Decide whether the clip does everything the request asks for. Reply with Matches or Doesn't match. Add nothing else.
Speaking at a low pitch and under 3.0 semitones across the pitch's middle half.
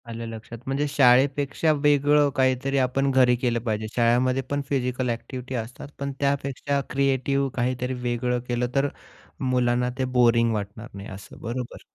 Matches